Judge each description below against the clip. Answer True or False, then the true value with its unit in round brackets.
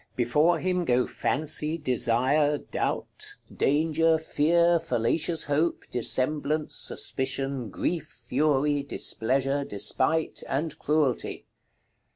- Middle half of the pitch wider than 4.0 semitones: False (3.3 semitones)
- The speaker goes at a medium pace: False (90 wpm)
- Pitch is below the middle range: False (145 Hz)